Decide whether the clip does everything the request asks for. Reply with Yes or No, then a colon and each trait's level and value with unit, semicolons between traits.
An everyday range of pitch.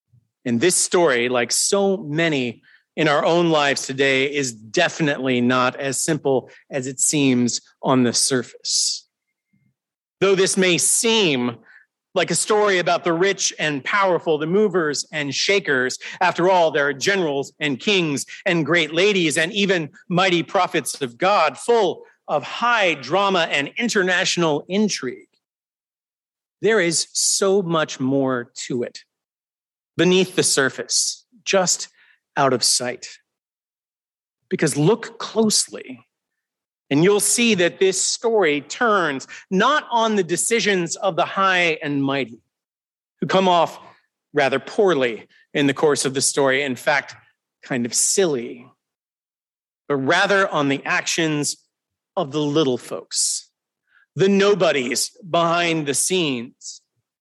No: wide, 5.9 semitones